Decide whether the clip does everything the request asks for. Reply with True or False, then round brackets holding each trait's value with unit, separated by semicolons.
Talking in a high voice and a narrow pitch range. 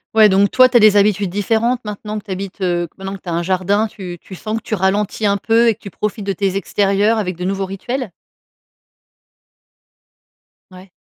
True (200 Hz; 2.1 semitones)